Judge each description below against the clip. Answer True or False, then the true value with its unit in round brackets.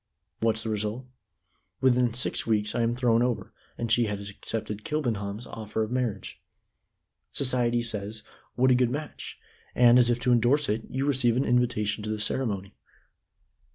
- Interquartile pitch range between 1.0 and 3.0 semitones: True (2.6 semitones)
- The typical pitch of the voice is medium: False (120 Hz)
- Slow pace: False (160 wpm)